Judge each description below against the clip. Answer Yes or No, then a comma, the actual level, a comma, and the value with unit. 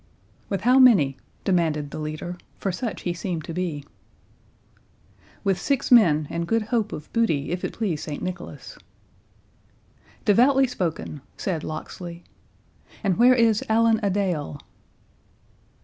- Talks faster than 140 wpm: No, slow, 135 wpm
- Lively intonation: Yes, wide, 6.0 semitones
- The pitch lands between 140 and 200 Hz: Yes, medium, 185 Hz